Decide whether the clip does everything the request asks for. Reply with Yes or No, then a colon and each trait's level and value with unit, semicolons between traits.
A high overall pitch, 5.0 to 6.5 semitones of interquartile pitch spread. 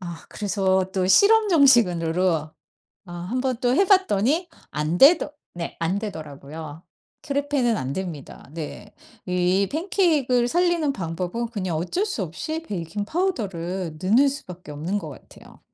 No: high, 195 Hz; wide, 8.5 semitones